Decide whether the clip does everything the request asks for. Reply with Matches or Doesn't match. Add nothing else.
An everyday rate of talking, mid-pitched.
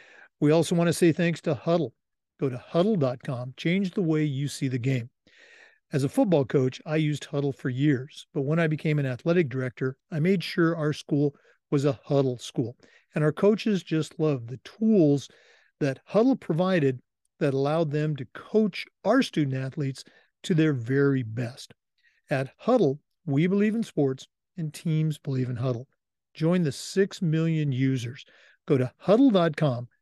Matches